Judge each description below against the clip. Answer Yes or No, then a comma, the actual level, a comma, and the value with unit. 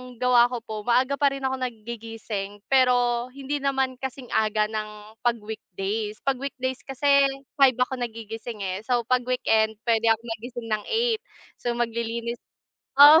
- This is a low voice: No, high, 240 Hz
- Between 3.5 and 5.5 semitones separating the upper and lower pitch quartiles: No, average, 2.8 semitones